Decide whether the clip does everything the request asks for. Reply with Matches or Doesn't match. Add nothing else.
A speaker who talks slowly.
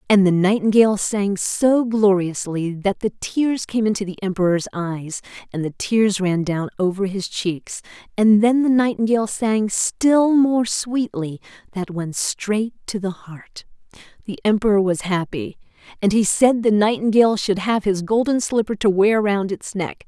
Doesn't match